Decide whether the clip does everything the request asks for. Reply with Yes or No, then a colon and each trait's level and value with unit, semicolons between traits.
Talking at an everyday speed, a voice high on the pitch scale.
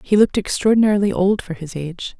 Yes: average, 190 wpm; high, 195 Hz